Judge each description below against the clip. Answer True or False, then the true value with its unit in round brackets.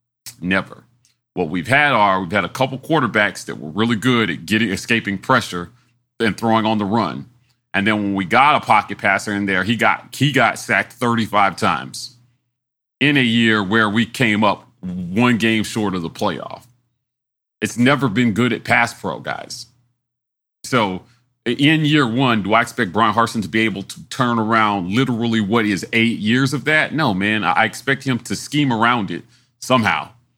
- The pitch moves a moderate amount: False (2.1 semitones)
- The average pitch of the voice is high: False (120 Hz)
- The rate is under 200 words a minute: True (185 wpm)